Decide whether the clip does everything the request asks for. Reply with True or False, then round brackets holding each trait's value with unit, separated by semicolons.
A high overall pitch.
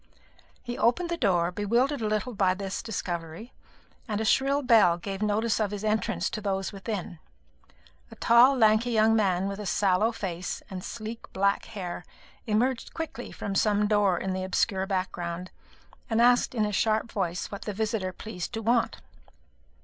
True (210 Hz)